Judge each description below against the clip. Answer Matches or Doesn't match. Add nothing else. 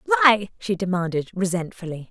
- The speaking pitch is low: Doesn't match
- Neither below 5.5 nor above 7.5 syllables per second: Doesn't match